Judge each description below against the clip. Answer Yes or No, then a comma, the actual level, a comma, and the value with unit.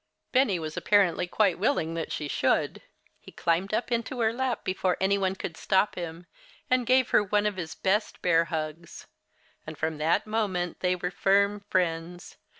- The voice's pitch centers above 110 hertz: Yes, medium, 185 Hz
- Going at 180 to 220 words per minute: No, average, 170 wpm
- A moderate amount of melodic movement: Yes, average, 3.9 semitones